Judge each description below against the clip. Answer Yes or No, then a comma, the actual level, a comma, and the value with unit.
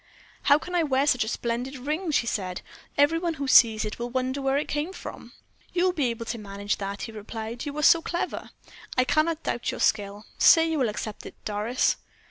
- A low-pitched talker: No, very high, 255 Hz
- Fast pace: Yes, fast, 220 wpm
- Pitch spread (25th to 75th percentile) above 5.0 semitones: Yes, wide, 5.6 semitones